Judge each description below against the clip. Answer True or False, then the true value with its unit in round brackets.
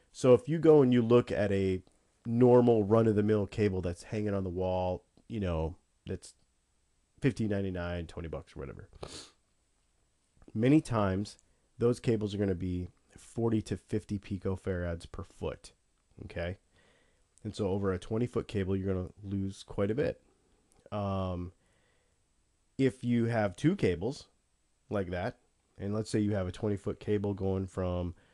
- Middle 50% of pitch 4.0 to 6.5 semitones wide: False (3.2 semitones)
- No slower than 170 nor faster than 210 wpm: False (160 wpm)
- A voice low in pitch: True (100 Hz)